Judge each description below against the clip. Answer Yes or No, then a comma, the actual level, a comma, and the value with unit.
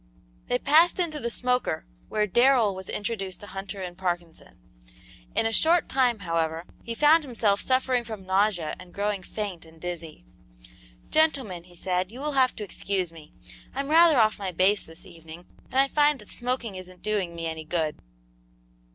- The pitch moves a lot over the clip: Yes, wide, 6.2 semitones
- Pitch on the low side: No, high, 205 Hz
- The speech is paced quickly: No, average, 175 wpm